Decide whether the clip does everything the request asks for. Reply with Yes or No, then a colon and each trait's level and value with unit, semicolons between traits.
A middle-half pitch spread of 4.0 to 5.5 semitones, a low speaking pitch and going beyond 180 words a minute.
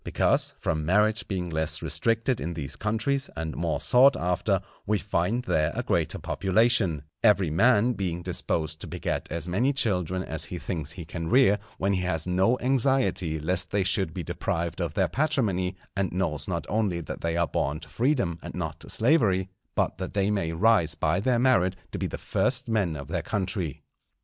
Yes: average, 4.9 semitones; very low, 95 Hz; average, 190 wpm